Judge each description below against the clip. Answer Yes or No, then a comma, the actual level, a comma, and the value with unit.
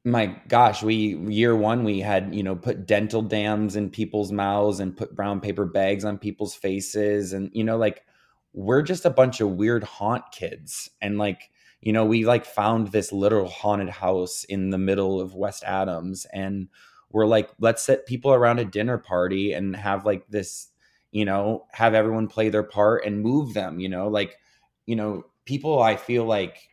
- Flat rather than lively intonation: Yes, narrow, 2.2 semitones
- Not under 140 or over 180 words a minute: No, average, 190 wpm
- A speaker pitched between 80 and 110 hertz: Yes, low, 105 Hz